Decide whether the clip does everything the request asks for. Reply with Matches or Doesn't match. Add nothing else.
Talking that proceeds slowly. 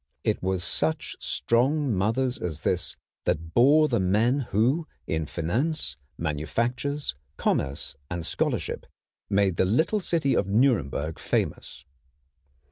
Matches